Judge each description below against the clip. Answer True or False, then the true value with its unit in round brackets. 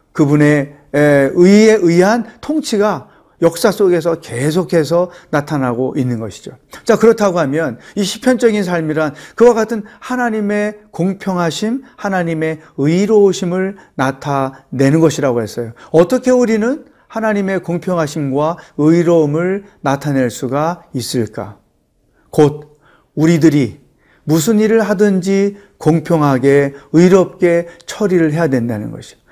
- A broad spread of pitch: True (5.8 semitones)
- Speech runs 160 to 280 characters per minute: True (270 characters per minute)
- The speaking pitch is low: False (170 Hz)